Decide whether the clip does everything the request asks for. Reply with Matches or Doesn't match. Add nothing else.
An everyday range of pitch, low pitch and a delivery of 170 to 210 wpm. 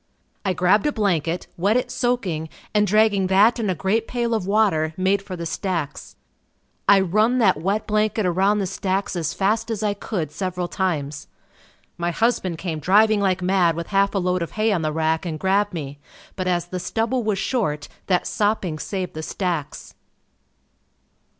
Doesn't match